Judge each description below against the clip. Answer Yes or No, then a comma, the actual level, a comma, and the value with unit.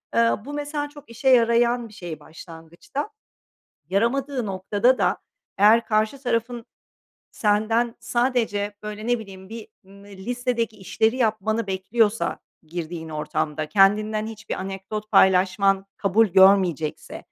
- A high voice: Yes, high, 215 Hz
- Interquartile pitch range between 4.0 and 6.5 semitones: No, average, 3.6 semitones